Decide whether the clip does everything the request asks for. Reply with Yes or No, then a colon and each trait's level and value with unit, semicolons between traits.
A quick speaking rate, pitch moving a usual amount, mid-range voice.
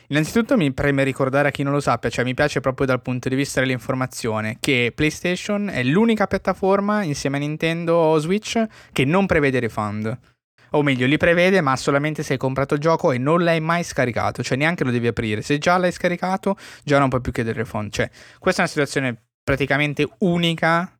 Yes: fast, 200 wpm; average, 4.8 semitones; medium, 145 Hz